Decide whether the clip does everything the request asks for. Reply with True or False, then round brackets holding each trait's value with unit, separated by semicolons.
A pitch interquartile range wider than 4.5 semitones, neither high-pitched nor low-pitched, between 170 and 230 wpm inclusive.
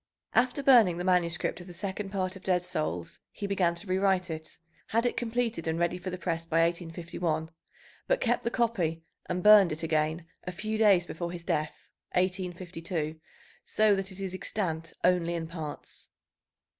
False (2.9 semitones; 180 Hz; 175 wpm)